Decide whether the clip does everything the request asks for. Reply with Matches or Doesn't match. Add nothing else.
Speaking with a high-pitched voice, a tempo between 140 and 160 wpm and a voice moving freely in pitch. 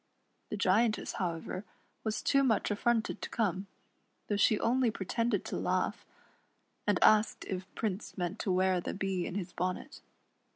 Doesn't match